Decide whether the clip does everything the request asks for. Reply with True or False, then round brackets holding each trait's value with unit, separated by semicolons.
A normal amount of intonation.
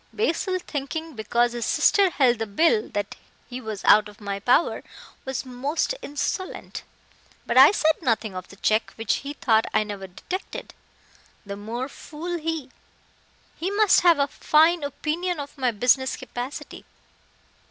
False (6.6 semitones)